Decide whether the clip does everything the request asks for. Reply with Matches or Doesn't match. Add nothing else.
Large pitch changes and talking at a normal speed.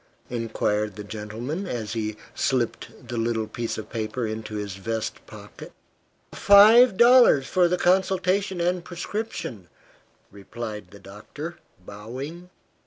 Doesn't match